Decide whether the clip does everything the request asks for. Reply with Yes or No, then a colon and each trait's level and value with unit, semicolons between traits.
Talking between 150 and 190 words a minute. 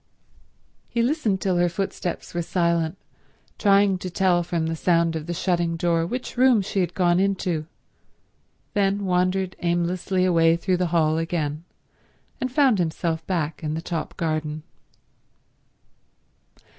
No: average, 140 wpm